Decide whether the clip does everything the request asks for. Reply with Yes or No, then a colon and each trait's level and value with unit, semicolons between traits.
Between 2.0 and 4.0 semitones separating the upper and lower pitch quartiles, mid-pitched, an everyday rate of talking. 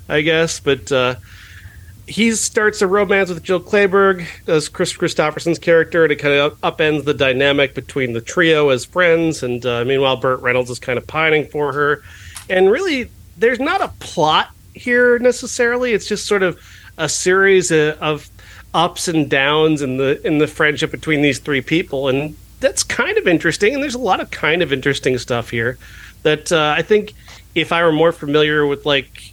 No: average, 5.1 semitones; medium, 150 Hz; average, 185 wpm